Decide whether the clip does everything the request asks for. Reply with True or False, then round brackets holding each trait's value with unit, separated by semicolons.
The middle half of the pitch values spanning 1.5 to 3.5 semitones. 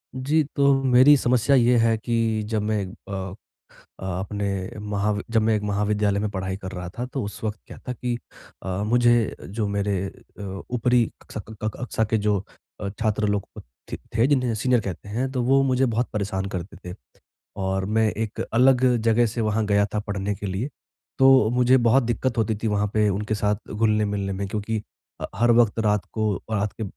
True (2.8 semitones)